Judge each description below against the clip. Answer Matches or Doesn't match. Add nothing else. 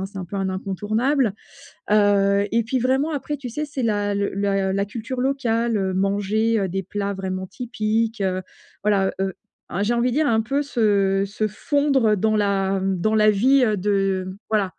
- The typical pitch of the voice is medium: Doesn't match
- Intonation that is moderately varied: Matches